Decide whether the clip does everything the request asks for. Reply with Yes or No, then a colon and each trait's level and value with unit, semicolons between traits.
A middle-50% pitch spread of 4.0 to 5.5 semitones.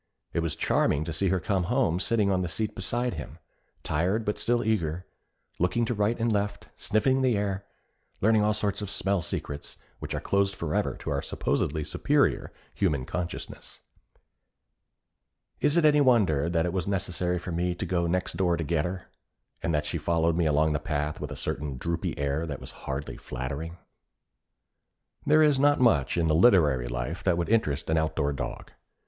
Yes: average, 4.8 semitones